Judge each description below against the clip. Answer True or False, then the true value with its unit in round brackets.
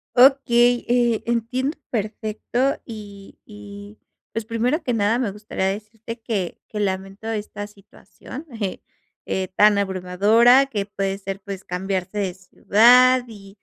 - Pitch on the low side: False (210 Hz)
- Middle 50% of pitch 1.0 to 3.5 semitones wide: True (3.2 semitones)